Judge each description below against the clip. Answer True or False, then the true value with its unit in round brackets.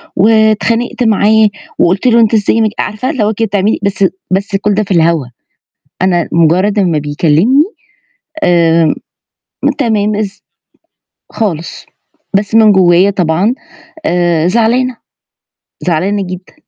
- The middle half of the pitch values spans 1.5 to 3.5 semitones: False (3.9 semitones)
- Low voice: False (200 Hz)